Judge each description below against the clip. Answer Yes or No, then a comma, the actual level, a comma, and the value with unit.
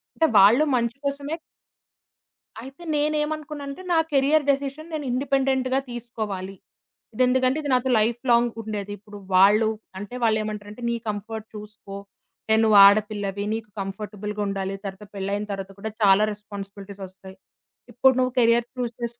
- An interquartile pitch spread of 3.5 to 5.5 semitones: Yes, average, 4.4 semitones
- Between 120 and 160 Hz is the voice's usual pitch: No, high, 220 Hz